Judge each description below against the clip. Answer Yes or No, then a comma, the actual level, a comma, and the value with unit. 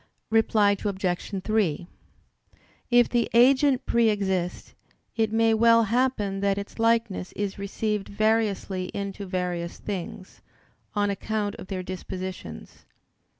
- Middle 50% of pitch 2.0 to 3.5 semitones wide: Yes, average, 3.0 semitones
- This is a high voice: Yes, high, 205 Hz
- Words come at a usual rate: No, slow, 115 wpm